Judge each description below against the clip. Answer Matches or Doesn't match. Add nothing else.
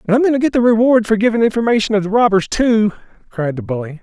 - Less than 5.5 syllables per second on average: Doesn't match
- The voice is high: Matches